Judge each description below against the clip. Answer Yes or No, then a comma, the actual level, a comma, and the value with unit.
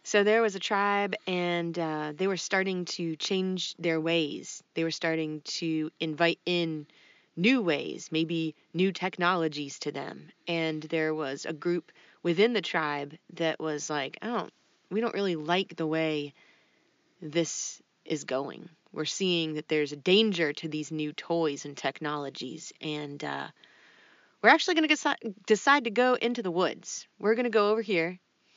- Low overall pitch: No, medium, 165 Hz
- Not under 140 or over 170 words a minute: Yes, average, 165 wpm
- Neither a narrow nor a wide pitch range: Yes, average, 3.7 semitones